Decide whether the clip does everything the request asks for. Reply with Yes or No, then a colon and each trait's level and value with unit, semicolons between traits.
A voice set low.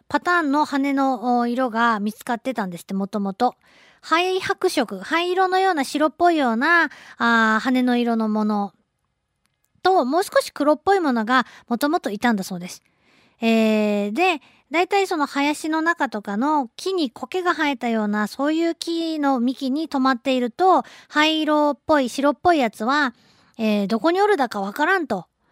No: very high, 275 Hz